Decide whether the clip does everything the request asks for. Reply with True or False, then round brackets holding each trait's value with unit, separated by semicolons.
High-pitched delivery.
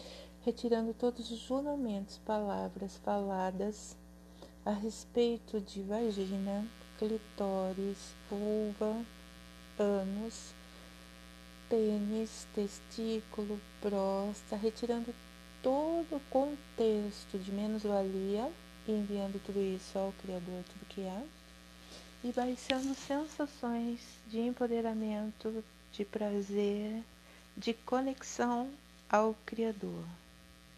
True (210 Hz)